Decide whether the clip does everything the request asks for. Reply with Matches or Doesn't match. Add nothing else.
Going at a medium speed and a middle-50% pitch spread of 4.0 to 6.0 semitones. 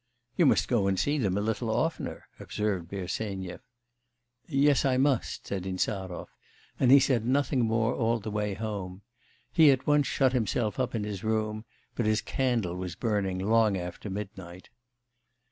Matches